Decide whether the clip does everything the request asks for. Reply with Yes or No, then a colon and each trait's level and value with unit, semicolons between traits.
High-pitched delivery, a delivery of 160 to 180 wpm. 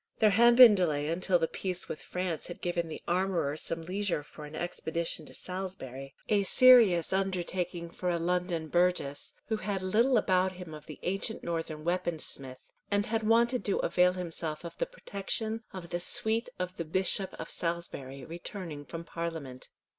No: medium, 180 Hz; average, 175 wpm